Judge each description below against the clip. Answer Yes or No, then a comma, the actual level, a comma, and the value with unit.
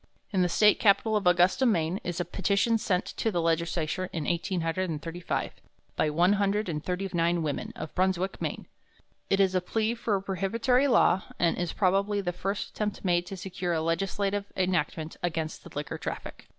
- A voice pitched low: No, medium, 185 Hz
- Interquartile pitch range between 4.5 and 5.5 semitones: No, average, 2.8 semitones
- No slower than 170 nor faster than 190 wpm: Yes, average, 180 wpm